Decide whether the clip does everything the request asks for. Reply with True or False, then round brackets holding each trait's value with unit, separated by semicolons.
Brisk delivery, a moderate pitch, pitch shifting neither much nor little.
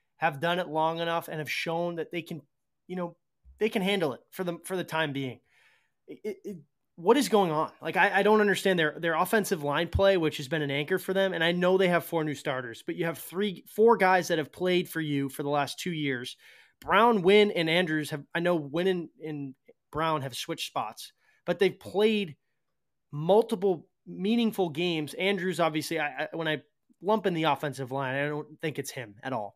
True (220 wpm; 170 Hz; 3.9 semitones)